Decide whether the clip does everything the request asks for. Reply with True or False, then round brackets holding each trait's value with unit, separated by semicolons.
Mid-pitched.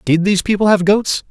False (195 Hz)